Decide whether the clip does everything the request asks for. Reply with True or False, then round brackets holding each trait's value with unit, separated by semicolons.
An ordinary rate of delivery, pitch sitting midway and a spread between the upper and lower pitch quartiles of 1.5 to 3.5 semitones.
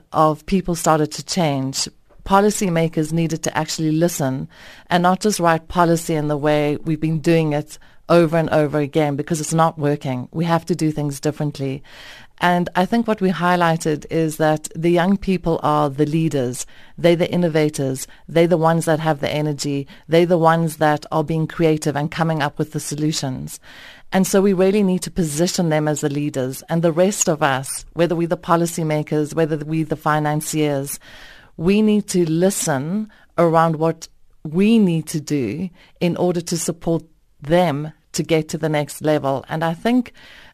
True (180 wpm; 160 Hz; 2.4 semitones)